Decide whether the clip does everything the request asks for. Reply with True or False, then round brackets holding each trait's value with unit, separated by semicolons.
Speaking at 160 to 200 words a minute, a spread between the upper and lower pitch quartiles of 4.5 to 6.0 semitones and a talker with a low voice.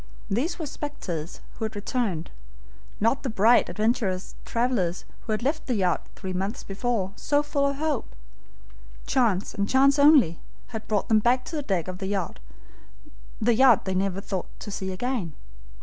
False (165 wpm; 5.4 semitones; 220 Hz)